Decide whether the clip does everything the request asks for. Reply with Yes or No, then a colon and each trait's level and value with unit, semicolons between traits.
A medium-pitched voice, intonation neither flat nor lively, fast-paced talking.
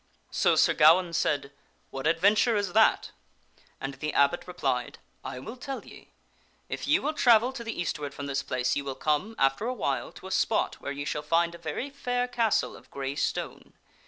No: medium, 165 Hz; wide, 7.9 semitones; fast, 225 wpm